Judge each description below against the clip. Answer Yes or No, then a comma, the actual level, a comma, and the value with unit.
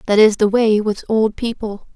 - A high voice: Yes, high, 215 Hz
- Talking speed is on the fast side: Yes, fast, 215 wpm